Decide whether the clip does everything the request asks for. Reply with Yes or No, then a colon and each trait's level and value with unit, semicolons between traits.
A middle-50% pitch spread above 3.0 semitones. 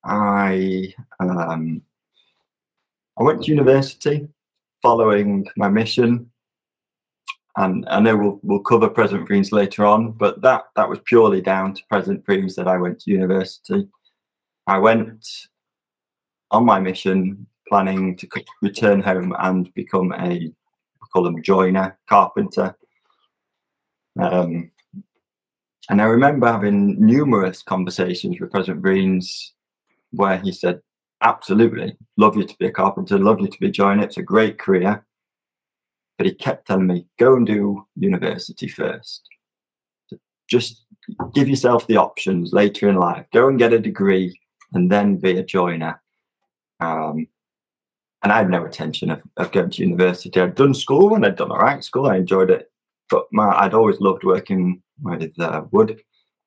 Yes: average, 4.4 semitones